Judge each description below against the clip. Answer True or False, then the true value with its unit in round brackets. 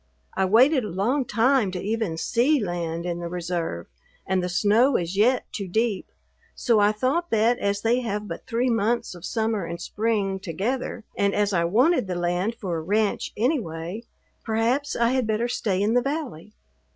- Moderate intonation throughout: True (4.8 semitones)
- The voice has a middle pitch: False (210 Hz)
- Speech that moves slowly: False (185 wpm)